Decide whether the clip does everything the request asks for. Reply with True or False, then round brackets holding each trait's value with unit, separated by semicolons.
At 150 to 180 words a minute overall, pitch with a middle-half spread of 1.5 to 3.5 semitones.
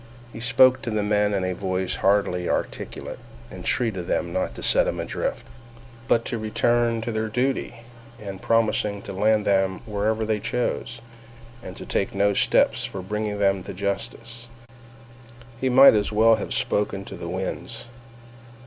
True (160 wpm; 2.8 semitones)